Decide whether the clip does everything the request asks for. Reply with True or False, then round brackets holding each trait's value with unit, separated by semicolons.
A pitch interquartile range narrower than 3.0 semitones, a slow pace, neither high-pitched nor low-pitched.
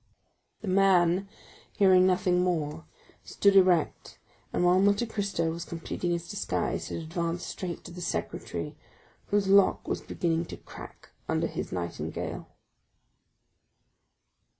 True (2.5 semitones; 125 wpm; 180 Hz)